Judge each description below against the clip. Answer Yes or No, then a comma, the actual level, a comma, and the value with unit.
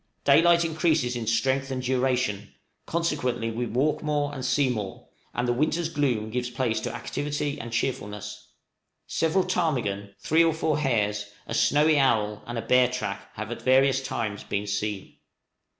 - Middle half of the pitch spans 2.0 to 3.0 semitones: No, average, 5.1 semitones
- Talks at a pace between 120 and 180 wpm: Yes, average, 160 wpm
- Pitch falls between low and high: No, low, 125 Hz